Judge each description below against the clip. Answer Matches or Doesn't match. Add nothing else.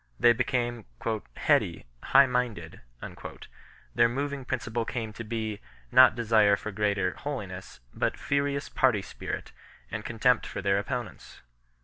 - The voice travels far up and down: Doesn't match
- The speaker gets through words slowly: Doesn't match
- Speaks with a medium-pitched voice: Doesn't match